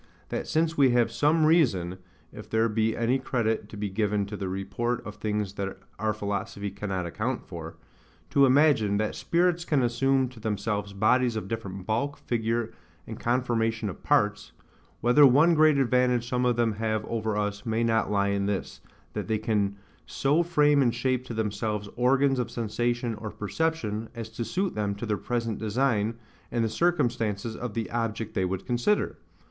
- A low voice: Yes, low, 115 Hz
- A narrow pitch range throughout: No, average, 3.3 semitones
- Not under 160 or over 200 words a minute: Yes, average, 175 wpm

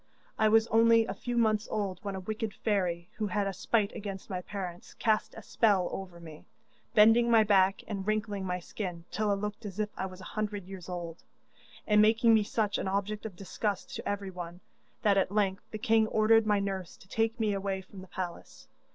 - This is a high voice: Yes, high, 205 Hz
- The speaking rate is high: Yes, fast, 210 wpm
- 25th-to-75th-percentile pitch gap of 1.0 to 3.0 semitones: Yes, narrow, 2.4 semitones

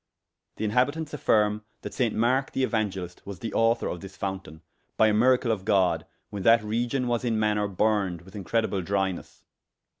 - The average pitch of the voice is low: Yes, low, 105 Hz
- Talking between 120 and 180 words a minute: Yes, average, 175 wpm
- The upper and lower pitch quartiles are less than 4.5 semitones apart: Yes, average, 3.3 semitones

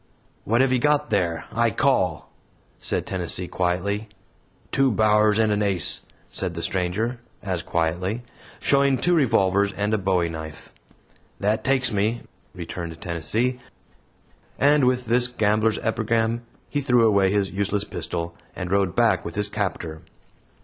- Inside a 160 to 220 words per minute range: No, average, 140 wpm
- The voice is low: Yes, low, 105 Hz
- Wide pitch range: No, average, 4.4 semitones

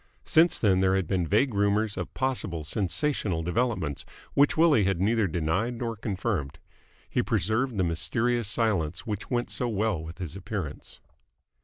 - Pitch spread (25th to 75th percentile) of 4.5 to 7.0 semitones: Yes, average, 5.0 semitones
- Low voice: Yes, low, 100 Hz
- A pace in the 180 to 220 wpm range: No, average, 155 wpm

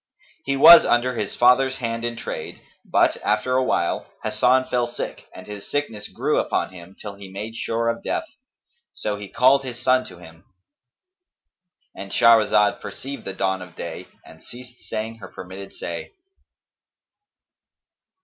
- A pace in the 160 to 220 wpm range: No, average, 150 wpm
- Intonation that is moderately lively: Yes, average, 4.3 semitones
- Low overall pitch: Yes, low, 115 Hz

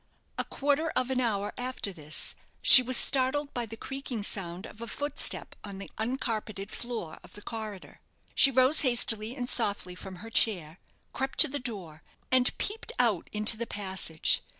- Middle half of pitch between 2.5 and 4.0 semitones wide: No, average, 4.4 semitones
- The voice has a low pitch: No, high, 225 Hz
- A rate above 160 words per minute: Yes, average, 175 wpm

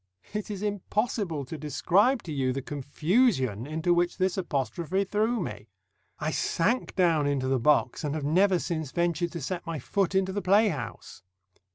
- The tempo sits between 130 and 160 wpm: No, average, 170 wpm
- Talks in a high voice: No, medium, 170 Hz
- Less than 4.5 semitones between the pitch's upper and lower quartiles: No, average, 5.2 semitones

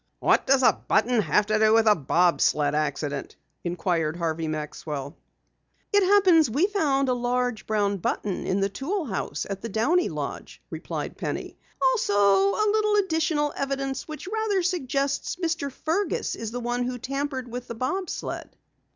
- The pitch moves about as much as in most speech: No, wide, 8.1 semitones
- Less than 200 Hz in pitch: No, high, 245 Hz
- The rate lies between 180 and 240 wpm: No, average, 170 wpm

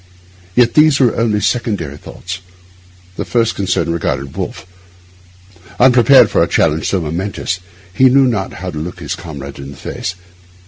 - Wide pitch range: Yes, wide, 6.8 semitones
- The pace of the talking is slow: No, average, 155 wpm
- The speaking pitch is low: Yes, very low, 95 Hz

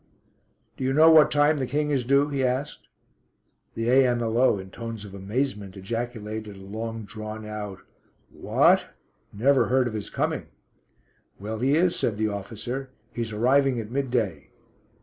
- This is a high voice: No, low, 115 Hz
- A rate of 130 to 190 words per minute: Yes, average, 150 wpm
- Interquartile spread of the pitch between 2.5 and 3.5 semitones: No, average, 3.9 semitones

